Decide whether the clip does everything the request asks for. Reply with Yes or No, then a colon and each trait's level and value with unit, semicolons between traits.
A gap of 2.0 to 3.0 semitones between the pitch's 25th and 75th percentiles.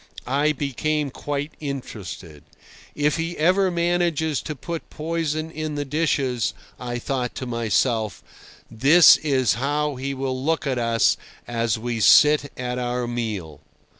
No: average, 4.1 semitones